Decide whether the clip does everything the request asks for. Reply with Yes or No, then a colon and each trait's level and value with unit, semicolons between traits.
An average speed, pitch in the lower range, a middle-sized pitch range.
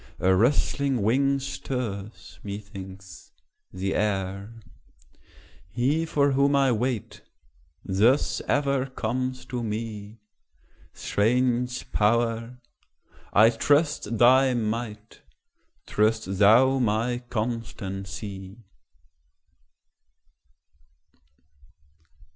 No: slow, 70 wpm; low, 115 Hz; average, 3.8 semitones